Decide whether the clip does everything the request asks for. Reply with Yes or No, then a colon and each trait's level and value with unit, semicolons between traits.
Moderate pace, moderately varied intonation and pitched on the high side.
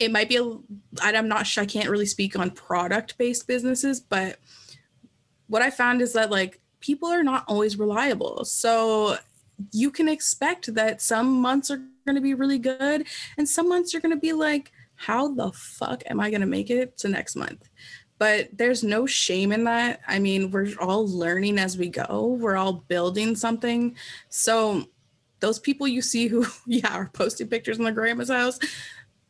Yes: average, 180 wpm; average, 4.1 semitones; high, 230 Hz